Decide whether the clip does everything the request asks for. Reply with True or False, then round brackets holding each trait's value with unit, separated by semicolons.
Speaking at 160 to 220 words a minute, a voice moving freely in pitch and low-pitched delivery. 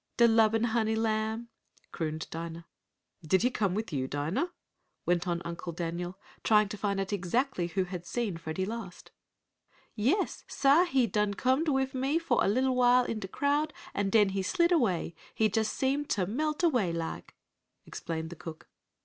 False (175 wpm; 6.3 semitones; 215 Hz)